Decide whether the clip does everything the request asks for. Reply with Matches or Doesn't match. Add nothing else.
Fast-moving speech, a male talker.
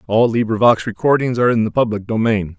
Doesn't match